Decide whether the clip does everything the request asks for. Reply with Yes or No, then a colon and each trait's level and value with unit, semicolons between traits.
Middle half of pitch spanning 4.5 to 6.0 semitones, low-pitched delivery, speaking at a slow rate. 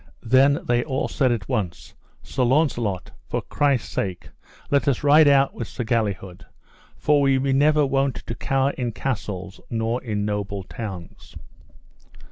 No: average, 4.9 semitones; low, 125 Hz; average, 150 wpm